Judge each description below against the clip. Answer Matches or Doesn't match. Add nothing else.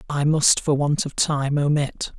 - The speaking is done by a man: Matches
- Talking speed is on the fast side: Doesn't match